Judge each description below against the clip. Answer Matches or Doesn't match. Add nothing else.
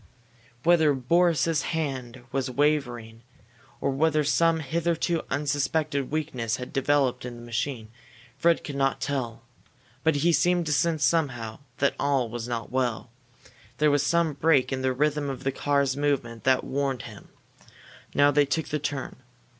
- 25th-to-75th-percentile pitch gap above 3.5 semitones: Doesn't match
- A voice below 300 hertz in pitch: Matches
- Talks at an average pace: Matches